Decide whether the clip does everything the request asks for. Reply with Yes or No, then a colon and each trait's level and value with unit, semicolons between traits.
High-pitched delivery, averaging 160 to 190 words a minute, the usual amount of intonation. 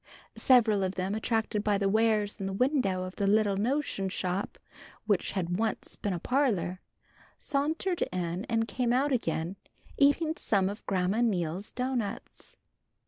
No: high, 205 Hz; average, 150 wpm; average, 4.5 semitones